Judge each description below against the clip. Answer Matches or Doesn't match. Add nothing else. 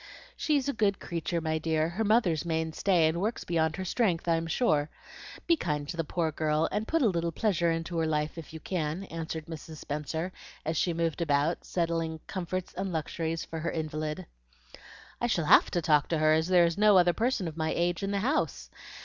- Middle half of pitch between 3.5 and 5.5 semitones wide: Doesn't match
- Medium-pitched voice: Matches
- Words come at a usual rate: Doesn't match